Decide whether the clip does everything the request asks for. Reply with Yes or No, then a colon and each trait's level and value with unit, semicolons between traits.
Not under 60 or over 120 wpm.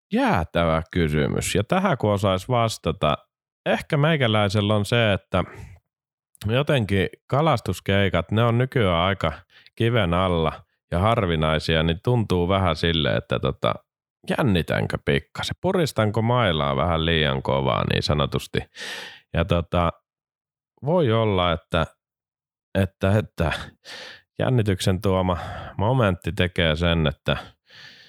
Yes: average, 105 wpm